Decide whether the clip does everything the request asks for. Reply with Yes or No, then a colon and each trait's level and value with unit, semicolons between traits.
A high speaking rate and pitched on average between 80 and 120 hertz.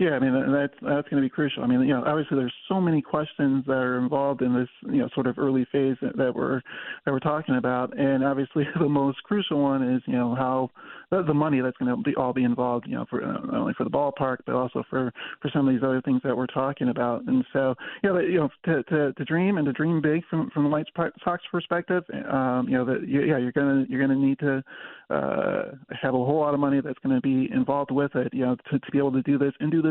No: fast, 275 wpm; medium, 140 Hz